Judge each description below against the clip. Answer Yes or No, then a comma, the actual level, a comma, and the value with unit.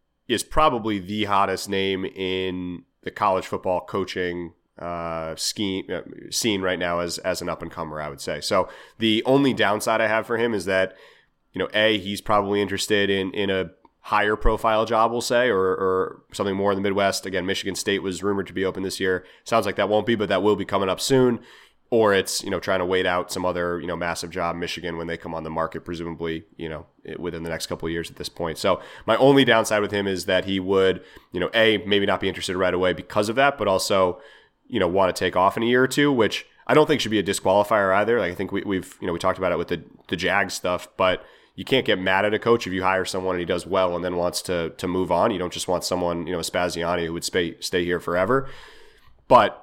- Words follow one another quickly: Yes, fast, 255 wpm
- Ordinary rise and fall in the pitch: Yes, average, 3.1 semitones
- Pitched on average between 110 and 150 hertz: No, very low, 95 Hz